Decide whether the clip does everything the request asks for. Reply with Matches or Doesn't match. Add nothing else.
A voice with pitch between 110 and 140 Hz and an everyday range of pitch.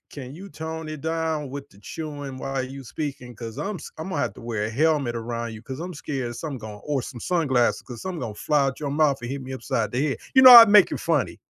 Matches